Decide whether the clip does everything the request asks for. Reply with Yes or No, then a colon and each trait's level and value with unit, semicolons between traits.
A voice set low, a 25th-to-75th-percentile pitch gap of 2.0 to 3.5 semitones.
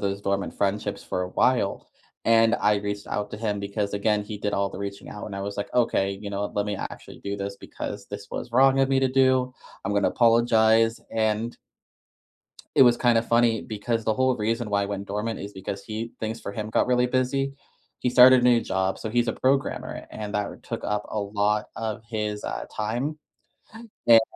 Yes: low, 110 Hz; average, 2.7 semitones